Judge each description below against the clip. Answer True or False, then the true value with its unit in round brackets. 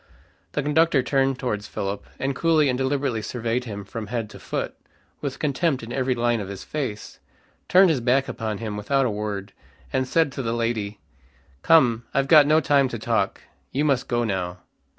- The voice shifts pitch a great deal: False (4.1 semitones)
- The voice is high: False (125 Hz)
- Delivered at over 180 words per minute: True (190 wpm)